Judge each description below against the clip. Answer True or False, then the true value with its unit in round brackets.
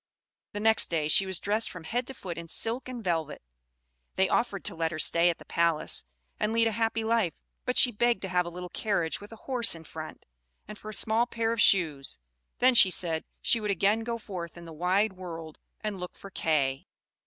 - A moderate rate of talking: False (220 wpm)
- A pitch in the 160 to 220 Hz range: True (190 Hz)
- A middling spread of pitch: True (5.0 semitones)